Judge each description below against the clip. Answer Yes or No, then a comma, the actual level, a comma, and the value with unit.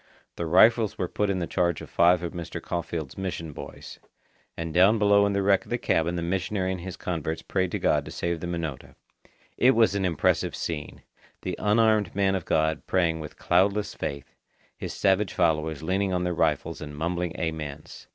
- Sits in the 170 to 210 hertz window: No, very low, 90 Hz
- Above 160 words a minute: Yes, average, 195 wpm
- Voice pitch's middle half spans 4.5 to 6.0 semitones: No, average, 3.2 semitones